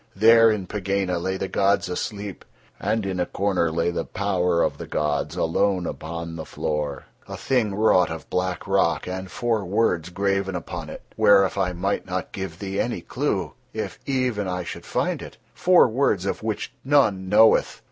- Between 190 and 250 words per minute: No, average, 175 wpm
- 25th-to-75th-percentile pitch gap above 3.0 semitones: No, narrow, 2.6 semitones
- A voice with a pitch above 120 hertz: No, very low, 95 Hz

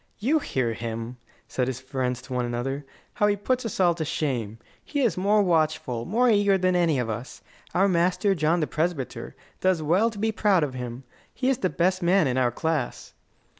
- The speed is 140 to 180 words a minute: No, fast, 205 wpm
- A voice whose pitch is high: No, medium, 165 Hz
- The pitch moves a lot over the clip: Yes, wide, 7.5 semitones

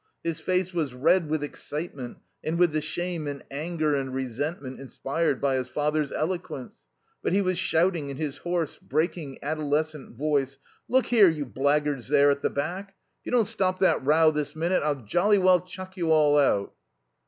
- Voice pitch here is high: No, medium, 155 Hz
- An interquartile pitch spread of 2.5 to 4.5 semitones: Yes, average, 3.7 semitones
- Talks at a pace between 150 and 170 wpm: No, average, 180 wpm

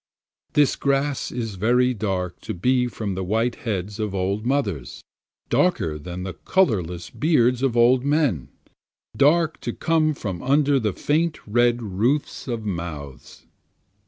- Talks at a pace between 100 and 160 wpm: Yes, average, 140 wpm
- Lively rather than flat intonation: Yes, wide, 6.5 semitones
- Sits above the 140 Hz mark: No, low, 120 Hz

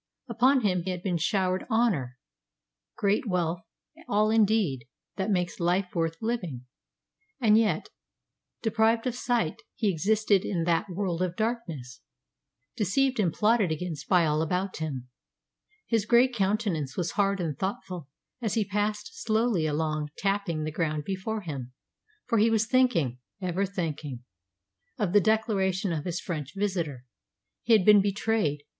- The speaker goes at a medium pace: Yes, average, 145 wpm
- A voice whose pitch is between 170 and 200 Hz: Yes, high, 190 Hz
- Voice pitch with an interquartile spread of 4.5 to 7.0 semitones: Yes, average, 4.9 semitones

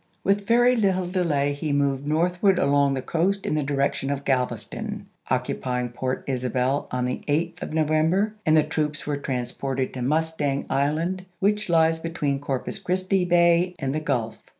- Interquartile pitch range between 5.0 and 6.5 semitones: No, average, 4.3 semitones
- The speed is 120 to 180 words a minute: Yes, average, 165 wpm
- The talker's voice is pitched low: No, medium, 150 Hz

